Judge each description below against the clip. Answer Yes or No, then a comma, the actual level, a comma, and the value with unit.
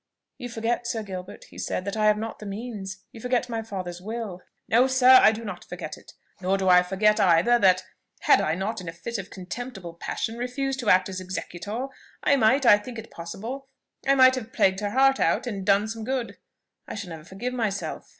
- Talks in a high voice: Yes, high, 215 Hz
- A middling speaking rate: No, fast, 220 wpm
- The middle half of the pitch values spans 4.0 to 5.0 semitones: Yes, average, 4.3 semitones